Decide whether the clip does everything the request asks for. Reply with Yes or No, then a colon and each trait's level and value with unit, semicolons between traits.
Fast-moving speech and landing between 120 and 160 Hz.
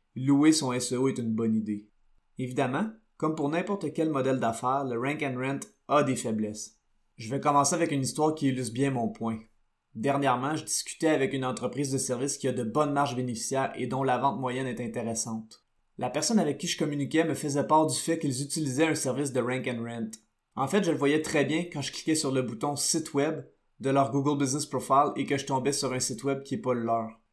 Yes: fast, 230 wpm; low, 135 Hz